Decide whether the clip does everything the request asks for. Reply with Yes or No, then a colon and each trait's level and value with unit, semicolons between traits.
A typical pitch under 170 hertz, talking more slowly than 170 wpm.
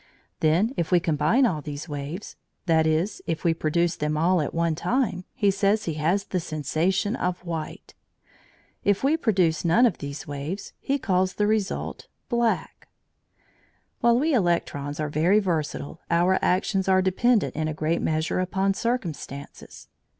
No: medium, 175 Hz; average, 155 wpm